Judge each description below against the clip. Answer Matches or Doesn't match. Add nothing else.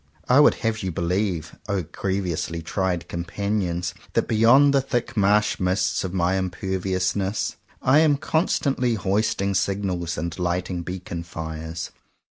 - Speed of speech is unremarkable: Doesn't match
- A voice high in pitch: Doesn't match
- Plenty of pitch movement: Doesn't match